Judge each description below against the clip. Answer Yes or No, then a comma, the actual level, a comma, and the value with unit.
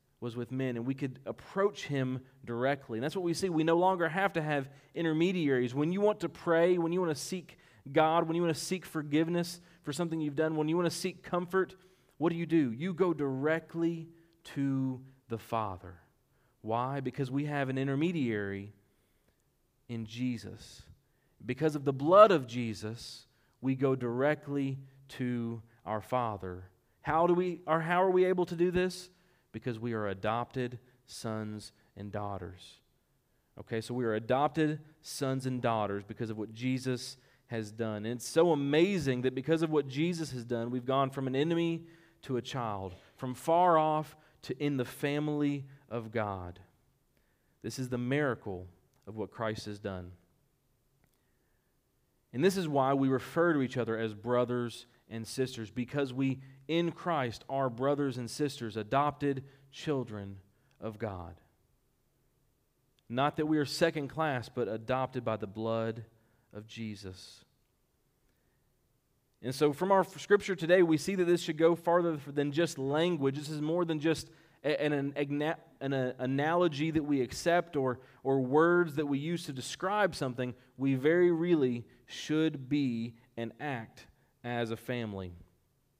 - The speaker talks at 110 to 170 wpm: Yes, average, 160 wpm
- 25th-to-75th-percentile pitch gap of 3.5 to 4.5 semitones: No, average, 5.1 semitones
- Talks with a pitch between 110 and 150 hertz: Yes, low, 135 Hz